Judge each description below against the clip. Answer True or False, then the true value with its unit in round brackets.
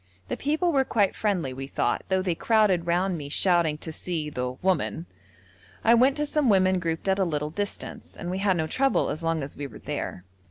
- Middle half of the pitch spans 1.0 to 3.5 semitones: False (4.6 semitones)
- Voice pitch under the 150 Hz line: False (180 Hz)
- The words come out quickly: True (215 wpm)